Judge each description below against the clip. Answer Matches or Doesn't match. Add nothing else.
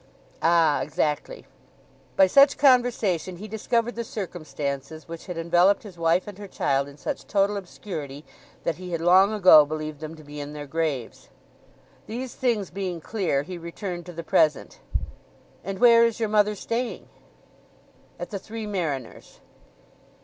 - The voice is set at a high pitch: Doesn't match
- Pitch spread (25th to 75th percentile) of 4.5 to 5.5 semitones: Matches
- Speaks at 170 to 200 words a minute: Doesn't match